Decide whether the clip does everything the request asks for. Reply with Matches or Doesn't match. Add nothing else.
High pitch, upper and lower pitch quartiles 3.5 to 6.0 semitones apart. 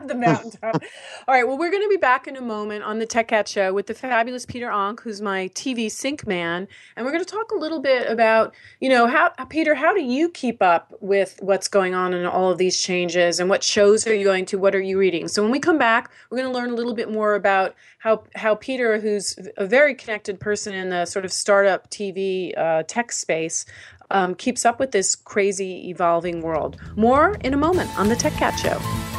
Matches